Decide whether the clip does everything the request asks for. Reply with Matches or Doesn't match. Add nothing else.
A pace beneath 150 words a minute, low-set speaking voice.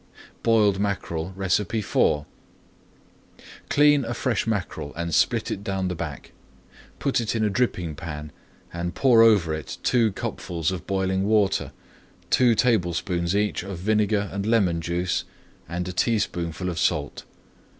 Matches